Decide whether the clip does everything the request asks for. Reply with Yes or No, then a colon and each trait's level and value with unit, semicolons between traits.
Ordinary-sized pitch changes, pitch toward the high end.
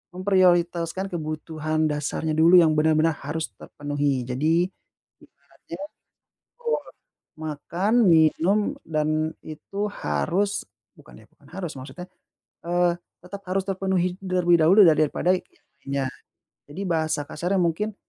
No: average, 3.1 semitones; medium, 165 Hz